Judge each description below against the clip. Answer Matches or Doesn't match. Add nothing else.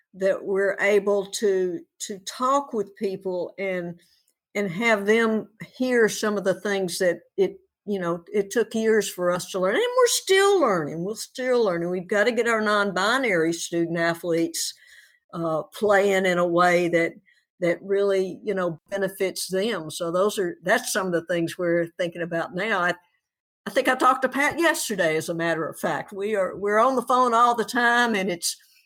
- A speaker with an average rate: Matches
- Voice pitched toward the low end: Doesn't match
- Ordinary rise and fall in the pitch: Matches